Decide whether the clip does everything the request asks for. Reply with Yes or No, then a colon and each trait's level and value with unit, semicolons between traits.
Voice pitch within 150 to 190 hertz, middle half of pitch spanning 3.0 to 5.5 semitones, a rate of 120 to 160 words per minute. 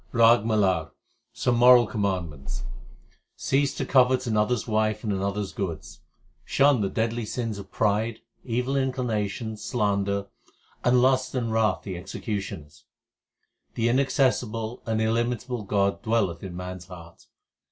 No: low, 110 Hz; average, 3.8 semitones; average, 140 wpm